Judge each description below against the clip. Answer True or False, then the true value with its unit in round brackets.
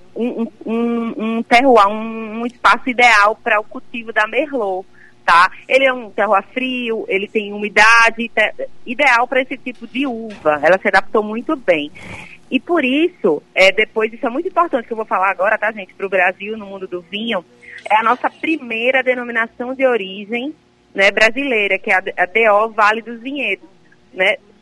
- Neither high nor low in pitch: False (225 Hz)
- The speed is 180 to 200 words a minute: True (185 wpm)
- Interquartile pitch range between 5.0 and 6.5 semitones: False (3.7 semitones)